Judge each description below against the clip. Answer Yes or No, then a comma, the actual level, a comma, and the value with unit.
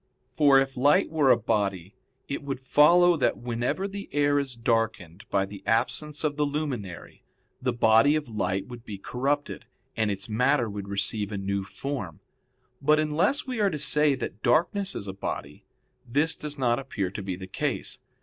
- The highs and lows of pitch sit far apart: Yes, wide, 6.3 semitones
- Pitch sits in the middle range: No, low, 125 Hz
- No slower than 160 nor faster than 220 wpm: Yes, average, 180 wpm